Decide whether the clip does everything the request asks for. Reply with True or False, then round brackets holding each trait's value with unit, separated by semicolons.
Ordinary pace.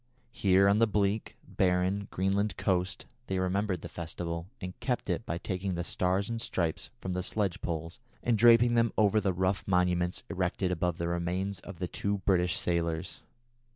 True (175 wpm)